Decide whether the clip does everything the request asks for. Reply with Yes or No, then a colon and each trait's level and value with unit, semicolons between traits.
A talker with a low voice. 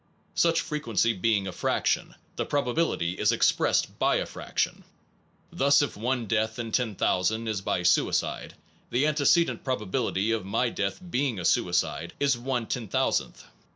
Yes: low, 115 Hz